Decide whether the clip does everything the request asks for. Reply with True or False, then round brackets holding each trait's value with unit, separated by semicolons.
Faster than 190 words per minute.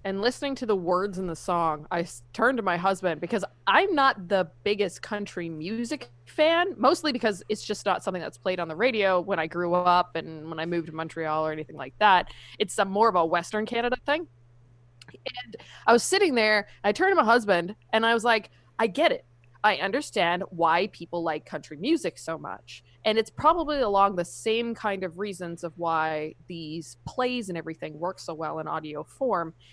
True (200 wpm)